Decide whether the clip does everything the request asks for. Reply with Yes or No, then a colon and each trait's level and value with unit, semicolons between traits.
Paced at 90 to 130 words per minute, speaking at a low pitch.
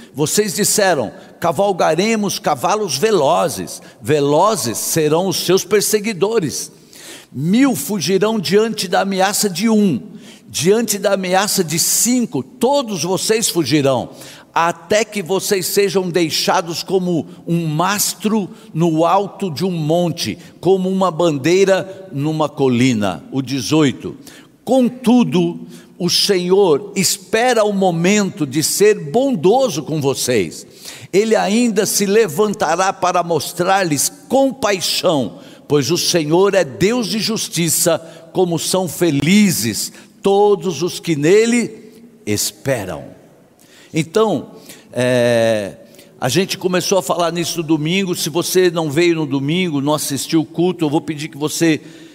No: slow, 120 wpm; medium, 185 Hz